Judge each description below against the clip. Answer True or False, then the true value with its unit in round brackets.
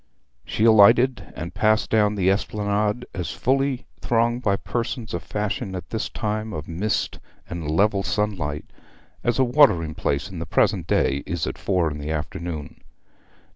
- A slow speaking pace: False (160 wpm)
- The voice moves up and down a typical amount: True (5.0 semitones)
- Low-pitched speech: True (105 Hz)